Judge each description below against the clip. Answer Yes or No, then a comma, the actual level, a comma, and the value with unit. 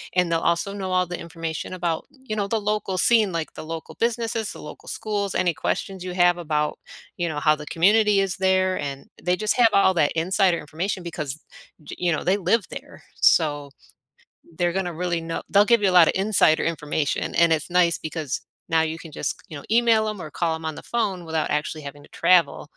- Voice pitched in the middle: Yes, medium, 175 Hz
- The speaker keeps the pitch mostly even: No, average, 3.6 semitones